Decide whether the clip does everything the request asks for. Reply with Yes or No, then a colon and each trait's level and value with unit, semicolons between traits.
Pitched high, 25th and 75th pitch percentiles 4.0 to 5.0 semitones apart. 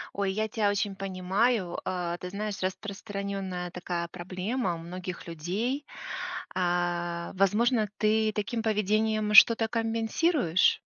No: high, 200 Hz; average, 3.4 semitones